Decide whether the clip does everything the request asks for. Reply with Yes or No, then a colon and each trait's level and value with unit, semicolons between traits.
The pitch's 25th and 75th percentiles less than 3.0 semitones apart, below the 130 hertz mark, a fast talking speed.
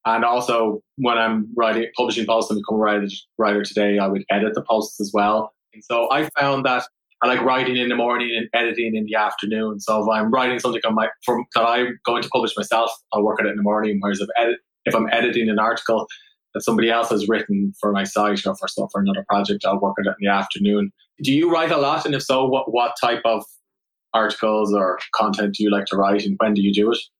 Yes: narrow, 2.5 semitones; low, 110 Hz; fast, 245 wpm